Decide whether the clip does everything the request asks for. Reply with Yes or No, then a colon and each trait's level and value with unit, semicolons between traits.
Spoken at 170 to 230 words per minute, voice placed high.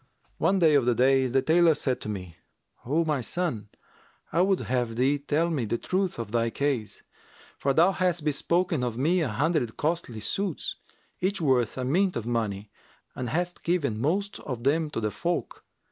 No: average, 190 wpm; medium, 140 Hz